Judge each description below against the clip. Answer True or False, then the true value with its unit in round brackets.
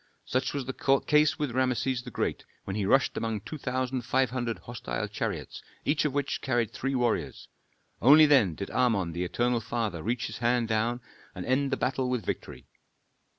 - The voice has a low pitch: True (125 Hz)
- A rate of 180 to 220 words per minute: True (185 wpm)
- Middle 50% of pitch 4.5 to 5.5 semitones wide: False (2.7 semitones)